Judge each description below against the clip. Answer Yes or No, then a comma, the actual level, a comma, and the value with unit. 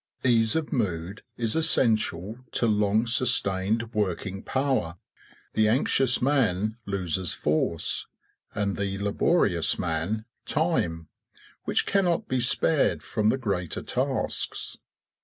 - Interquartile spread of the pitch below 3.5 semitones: No, average, 5.1 semitones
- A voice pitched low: Yes, low, 110 Hz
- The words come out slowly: Yes, slow, 110 wpm